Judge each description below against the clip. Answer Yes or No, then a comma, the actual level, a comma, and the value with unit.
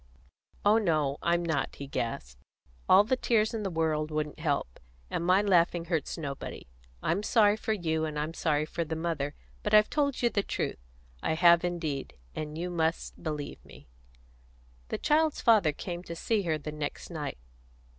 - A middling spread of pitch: Yes, average, 4.7 semitones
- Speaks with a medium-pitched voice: Yes, medium, 165 Hz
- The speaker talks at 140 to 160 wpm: No, average, 175 wpm